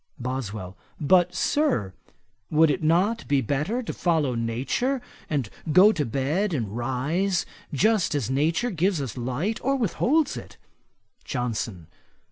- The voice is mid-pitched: Yes, medium, 150 Hz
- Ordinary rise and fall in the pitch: No, wide, 7.6 semitones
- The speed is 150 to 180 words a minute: No, slow, 135 wpm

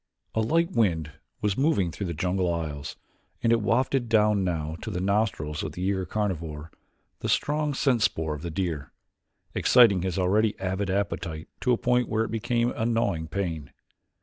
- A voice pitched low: Yes, low, 100 Hz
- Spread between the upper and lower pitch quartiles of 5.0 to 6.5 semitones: Yes, average, 5.3 semitones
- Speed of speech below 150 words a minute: No, average, 175 wpm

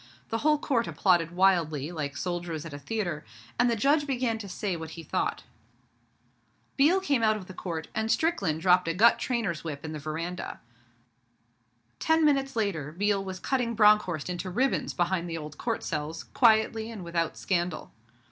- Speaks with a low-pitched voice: No, medium, 185 Hz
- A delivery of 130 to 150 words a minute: No, average, 175 wpm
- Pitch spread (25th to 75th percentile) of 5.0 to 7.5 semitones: Yes, wide, 5.6 semitones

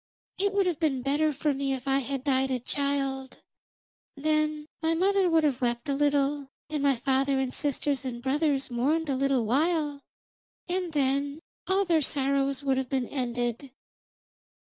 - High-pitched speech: Yes, very high, 280 Hz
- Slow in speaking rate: No, average, 165 wpm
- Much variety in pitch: No, narrow, 2.5 semitones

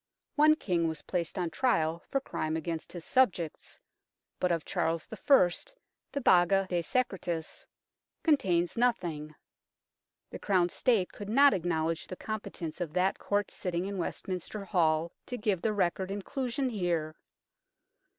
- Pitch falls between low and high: Yes, medium, 180 Hz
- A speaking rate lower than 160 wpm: Yes, average, 140 wpm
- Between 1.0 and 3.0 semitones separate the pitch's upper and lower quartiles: No, average, 4.2 semitones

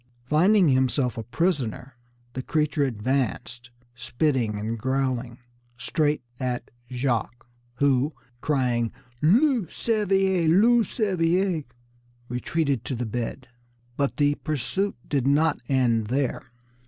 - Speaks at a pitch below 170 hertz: Yes, low, 135 Hz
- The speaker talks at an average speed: No, slow, 105 wpm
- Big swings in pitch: No, average, 4.8 semitones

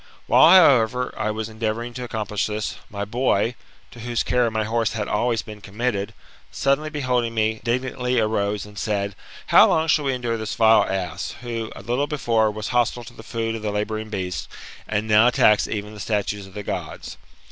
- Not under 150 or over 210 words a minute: Yes, average, 190 wpm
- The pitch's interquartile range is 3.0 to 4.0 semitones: No, narrow, 2.5 semitones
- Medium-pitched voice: No, low, 110 Hz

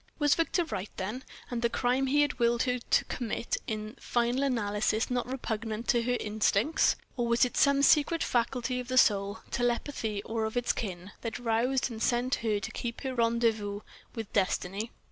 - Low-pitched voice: No, high, 235 Hz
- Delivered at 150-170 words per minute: No, average, 185 wpm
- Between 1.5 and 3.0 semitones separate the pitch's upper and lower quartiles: Yes, narrow, 2.6 semitones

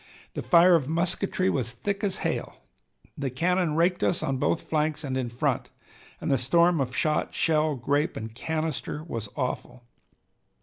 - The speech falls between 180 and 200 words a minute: No, average, 165 wpm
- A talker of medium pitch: Yes, medium, 155 Hz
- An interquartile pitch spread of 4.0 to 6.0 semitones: Yes, average, 4.8 semitones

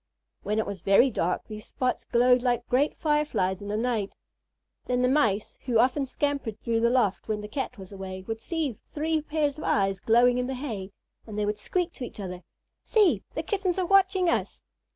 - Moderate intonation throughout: No, wide, 5.9 semitones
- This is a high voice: Yes, high, 245 Hz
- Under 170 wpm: No, fast, 205 wpm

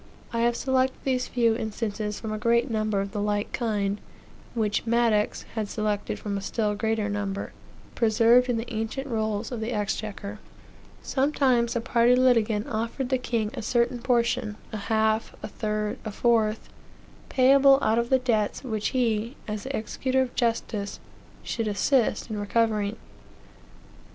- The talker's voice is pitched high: Yes, high, 225 Hz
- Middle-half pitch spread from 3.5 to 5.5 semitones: No, narrow, 2.4 semitones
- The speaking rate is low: No, average, 155 wpm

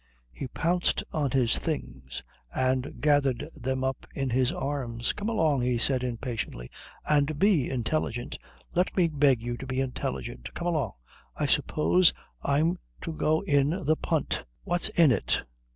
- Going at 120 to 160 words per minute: Yes, average, 150 wpm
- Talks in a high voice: No, medium, 140 Hz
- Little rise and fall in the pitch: No, average, 3.8 semitones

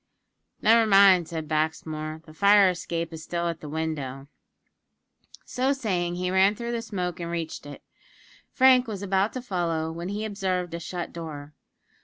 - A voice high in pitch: No, medium, 175 Hz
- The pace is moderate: Yes, average, 165 wpm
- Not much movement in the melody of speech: No, average, 3.9 semitones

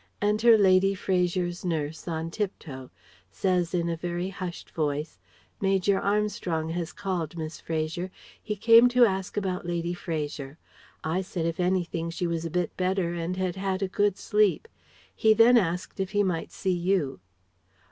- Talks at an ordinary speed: Yes, average, 160 wpm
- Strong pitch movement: No, average, 2.8 semitones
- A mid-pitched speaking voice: Yes, medium, 180 Hz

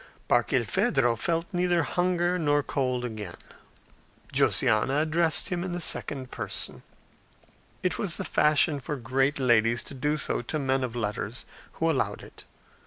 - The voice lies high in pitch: No, medium, 140 Hz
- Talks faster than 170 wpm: No, average, 145 wpm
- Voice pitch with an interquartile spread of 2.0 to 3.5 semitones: No, average, 5.1 semitones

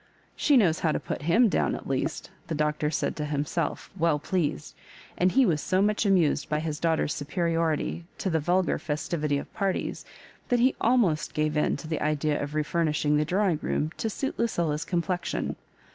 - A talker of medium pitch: Yes, medium, 165 Hz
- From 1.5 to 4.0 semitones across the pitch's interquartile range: Yes, average, 3.6 semitones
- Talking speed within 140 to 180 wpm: No, average, 190 wpm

